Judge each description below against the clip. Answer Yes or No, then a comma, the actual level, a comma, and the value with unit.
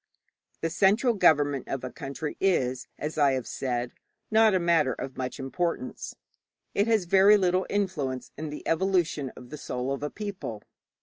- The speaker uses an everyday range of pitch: No, wide, 6.2 semitones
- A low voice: No, medium, 155 Hz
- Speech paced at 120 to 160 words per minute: No, average, 170 wpm